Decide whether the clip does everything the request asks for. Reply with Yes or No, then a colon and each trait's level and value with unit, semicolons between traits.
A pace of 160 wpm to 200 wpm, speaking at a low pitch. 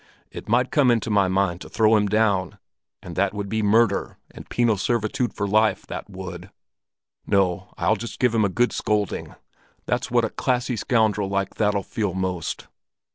Yes: average, 180 wpm; low, 105 Hz